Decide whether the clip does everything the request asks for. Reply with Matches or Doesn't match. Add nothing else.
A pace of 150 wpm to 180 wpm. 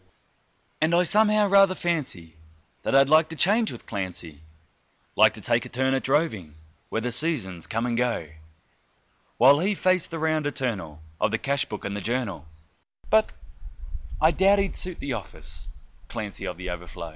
Matches